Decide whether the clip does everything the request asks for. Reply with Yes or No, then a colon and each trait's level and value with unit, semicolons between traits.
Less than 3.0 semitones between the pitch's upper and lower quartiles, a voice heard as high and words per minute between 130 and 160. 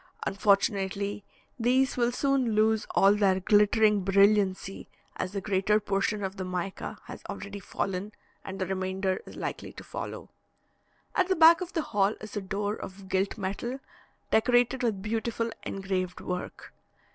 Yes: narrow, 2.6 semitones; high, 205 Hz; average, 150 wpm